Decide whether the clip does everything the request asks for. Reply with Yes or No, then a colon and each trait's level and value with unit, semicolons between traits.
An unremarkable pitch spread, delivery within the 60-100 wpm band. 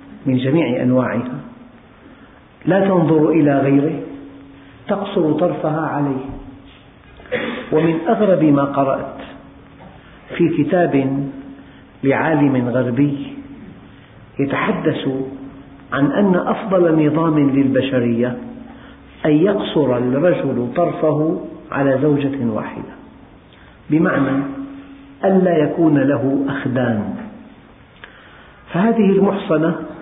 Yes: average, 4.1 semitones; average, 75 wpm